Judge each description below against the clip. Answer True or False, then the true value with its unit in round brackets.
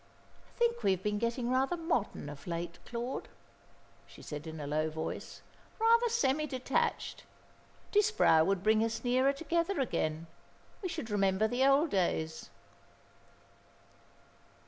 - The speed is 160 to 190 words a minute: False (135 wpm)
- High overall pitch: True (235 Hz)